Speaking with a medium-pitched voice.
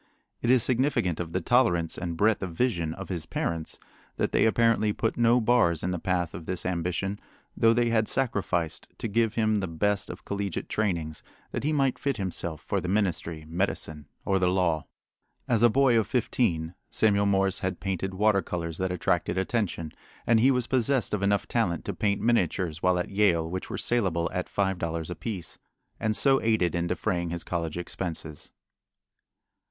No: very low, 95 Hz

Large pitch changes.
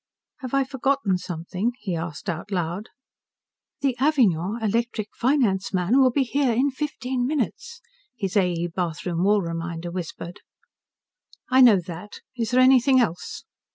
Yes: wide, 6.5 semitones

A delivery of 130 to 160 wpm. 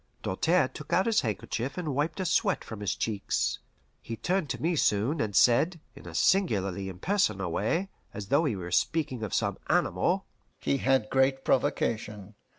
No: average, 170 wpm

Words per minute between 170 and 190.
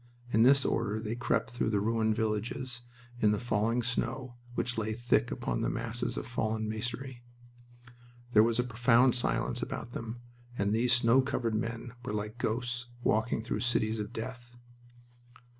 No: average, 160 wpm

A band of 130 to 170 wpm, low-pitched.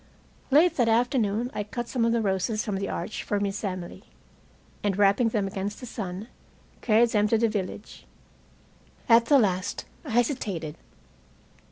No: average, 160 wpm; high, 215 Hz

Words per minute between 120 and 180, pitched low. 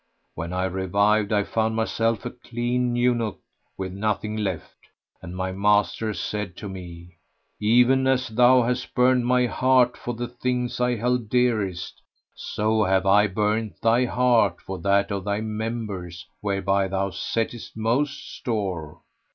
Yes: average, 145 wpm; low, 110 Hz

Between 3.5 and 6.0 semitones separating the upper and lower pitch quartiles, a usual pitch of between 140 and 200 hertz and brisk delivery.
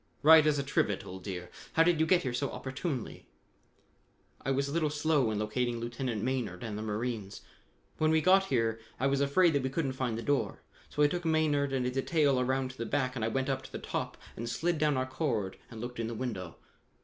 No: average, 4.1 semitones; low, 130 Hz; fast, 235 wpm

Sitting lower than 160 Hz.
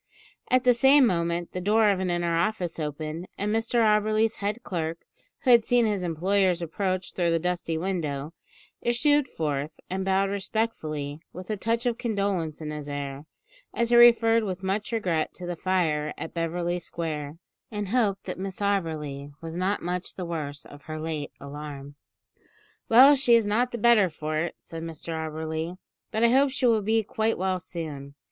No: medium, 180 Hz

